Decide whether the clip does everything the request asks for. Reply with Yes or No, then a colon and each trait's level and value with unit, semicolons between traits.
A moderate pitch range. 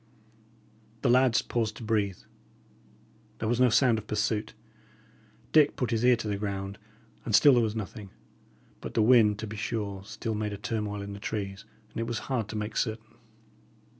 No: narrow, 2.0 semitones